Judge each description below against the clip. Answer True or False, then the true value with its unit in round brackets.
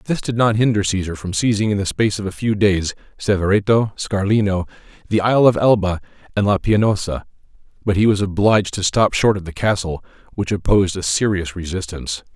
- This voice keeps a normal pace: True (185 wpm)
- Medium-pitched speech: False (100 Hz)